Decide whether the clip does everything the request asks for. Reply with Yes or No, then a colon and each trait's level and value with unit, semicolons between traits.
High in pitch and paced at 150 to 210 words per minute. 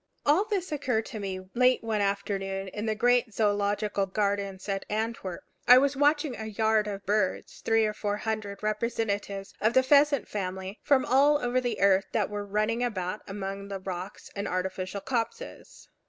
Yes: high, 210 Hz; average, 170 wpm